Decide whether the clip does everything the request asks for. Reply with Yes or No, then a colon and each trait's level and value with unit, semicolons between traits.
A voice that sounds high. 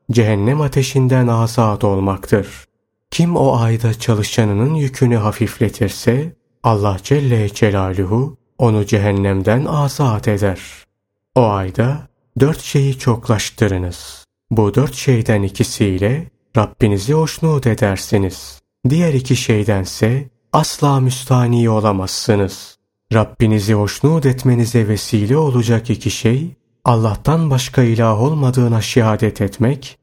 No: low, 115 Hz